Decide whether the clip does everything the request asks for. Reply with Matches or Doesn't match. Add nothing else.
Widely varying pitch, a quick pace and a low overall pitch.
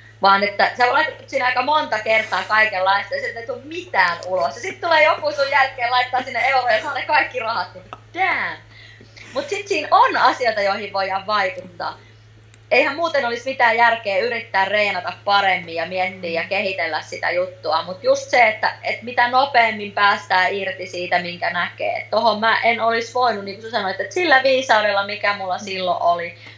Doesn't match